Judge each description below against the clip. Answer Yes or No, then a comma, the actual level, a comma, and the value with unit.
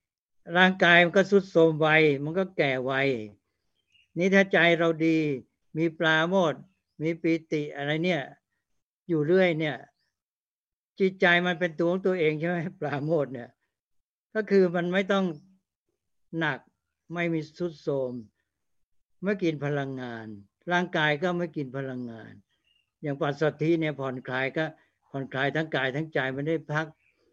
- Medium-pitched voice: Yes, medium, 155 Hz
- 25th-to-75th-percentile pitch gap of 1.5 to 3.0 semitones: No, average, 4.7 semitones